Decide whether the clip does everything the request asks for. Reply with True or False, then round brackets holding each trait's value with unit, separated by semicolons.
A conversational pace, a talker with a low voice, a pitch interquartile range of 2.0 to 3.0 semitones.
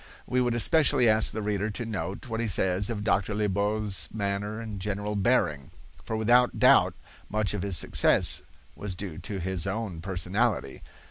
True (170 wpm; 105 Hz; 2.6 semitones)